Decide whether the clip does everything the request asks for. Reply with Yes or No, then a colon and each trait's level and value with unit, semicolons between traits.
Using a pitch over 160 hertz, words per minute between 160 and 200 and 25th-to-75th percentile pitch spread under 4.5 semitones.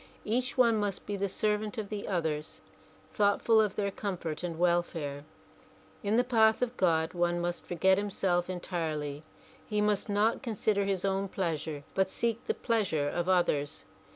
Yes: high, 190 Hz; average, 165 wpm; average, 3.6 semitones